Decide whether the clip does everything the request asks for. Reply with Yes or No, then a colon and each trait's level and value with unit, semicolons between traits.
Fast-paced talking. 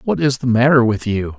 Yes: fast, 260 wpm